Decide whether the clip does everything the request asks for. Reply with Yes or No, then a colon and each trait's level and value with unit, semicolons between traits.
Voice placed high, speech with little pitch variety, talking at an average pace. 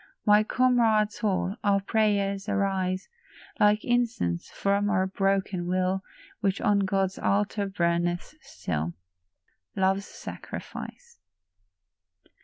No: high, 195 Hz; narrow, 1.9 semitones; slow, 95 wpm